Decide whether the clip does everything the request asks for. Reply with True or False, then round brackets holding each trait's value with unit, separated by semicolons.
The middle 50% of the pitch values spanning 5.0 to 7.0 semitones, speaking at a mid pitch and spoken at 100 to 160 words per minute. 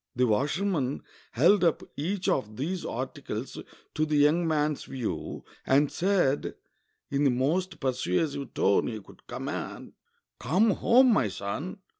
True (5.6 semitones; 145 Hz; 135 wpm)